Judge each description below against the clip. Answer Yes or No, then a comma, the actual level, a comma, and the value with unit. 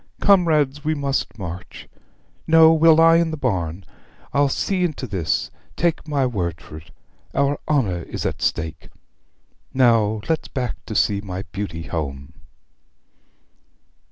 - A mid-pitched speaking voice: No, low, 125 Hz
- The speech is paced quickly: No, slow, 135 wpm